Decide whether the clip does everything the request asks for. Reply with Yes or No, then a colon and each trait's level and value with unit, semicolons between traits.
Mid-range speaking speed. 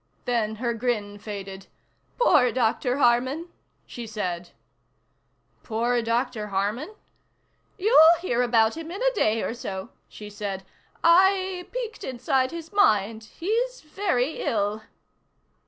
No: slow, 120 wpm